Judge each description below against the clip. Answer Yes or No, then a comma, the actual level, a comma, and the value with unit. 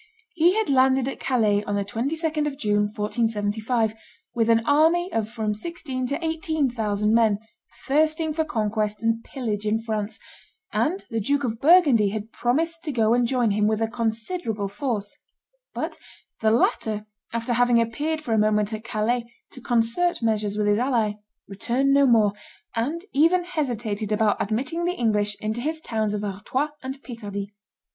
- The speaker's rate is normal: Yes, average, 165 wpm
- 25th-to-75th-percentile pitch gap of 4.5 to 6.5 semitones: Yes, average, 4.8 semitones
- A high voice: Yes, high, 230 Hz